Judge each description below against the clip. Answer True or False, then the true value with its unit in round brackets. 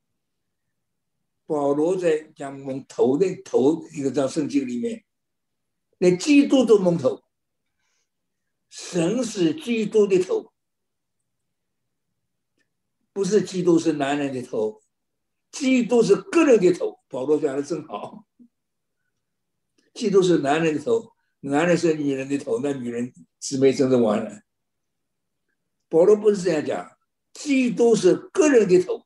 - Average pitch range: False (8.7 semitones)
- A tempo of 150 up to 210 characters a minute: True (180 characters per minute)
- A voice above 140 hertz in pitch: True (185 Hz)